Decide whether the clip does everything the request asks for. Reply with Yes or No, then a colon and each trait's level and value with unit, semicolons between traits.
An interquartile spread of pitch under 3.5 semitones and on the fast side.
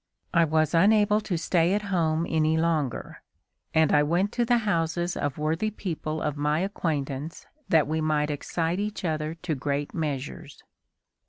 No: average, 2.9 semitones; average, 160 wpm